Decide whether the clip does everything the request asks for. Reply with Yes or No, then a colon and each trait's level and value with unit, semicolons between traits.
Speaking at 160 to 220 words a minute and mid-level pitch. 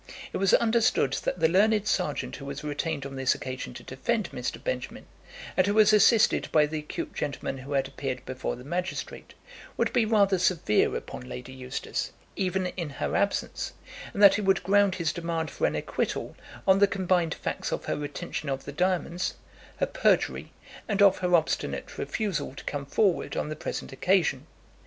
Yes: average, 185 wpm; medium, 175 Hz